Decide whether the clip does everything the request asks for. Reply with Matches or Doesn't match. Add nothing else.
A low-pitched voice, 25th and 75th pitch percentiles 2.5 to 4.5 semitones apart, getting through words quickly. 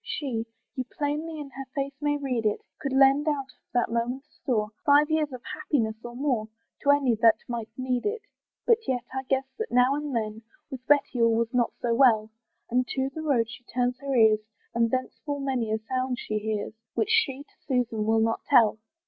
Doesn't match